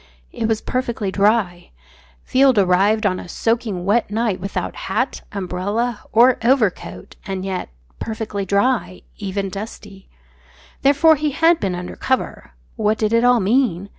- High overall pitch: Yes, high, 215 Hz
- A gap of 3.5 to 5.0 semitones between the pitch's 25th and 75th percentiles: Yes, average, 3.8 semitones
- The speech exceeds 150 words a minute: No, average, 140 wpm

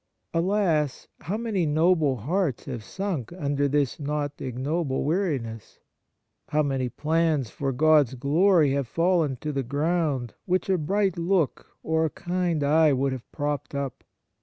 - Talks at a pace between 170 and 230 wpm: No, average, 145 wpm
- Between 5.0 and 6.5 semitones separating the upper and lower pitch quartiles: No, average, 3.9 semitones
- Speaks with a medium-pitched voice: Yes, medium, 150 Hz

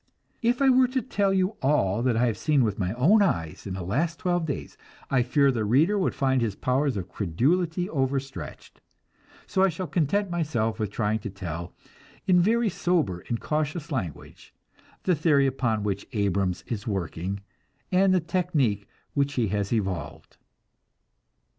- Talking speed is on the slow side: No, average, 165 wpm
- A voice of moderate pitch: No, low, 130 Hz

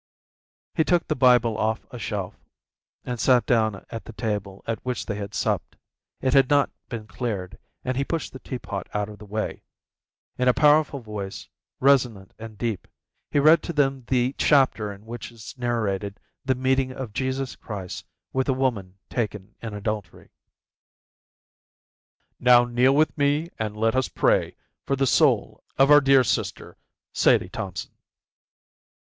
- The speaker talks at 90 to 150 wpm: No, average, 160 wpm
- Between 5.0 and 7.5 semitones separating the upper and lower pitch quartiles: No, average, 4.0 semitones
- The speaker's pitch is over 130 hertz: No, low, 120 Hz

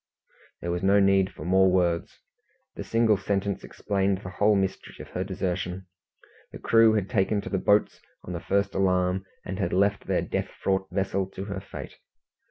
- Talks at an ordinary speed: Yes, average, 180 wpm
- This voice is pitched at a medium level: No, very low, 95 Hz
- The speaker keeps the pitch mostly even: Yes, narrow, 1.4 semitones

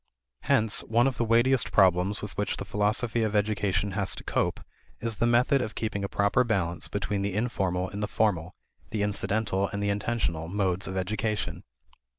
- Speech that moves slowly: No, average, 180 wpm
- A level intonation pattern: Yes, narrow, 2.3 semitones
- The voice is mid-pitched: No, low, 105 Hz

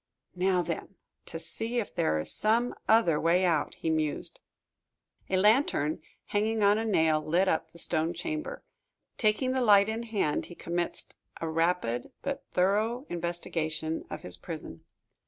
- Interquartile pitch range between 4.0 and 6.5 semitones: Yes, average, 5.3 semitones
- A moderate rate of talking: Yes, average, 155 wpm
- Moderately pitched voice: Yes, medium, 180 Hz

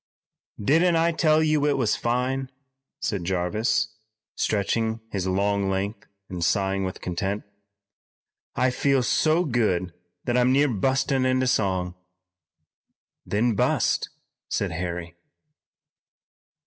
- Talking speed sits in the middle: No, slow, 110 wpm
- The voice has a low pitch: Yes, low, 110 Hz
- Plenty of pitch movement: Yes, wide, 5.7 semitones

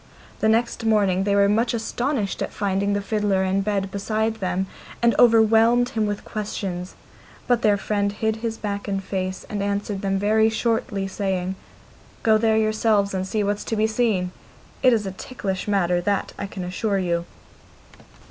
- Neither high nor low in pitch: No, high, 205 Hz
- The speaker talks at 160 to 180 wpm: Yes, average, 175 wpm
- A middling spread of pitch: No, narrow, 2.2 semitones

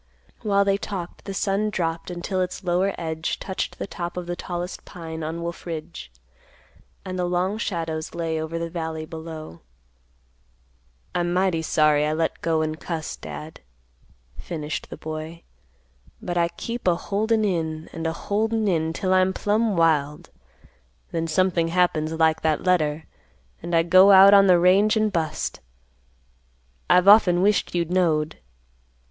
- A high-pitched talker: No, medium, 170 Hz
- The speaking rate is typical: Yes, average, 155 wpm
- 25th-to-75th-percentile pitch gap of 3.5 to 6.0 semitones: No, average, 2.7 semitones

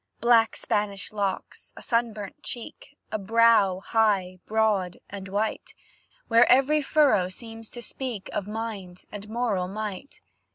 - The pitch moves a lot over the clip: No, average, 3.0 semitones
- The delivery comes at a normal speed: No, slow, 130 wpm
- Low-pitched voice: No, high, 215 Hz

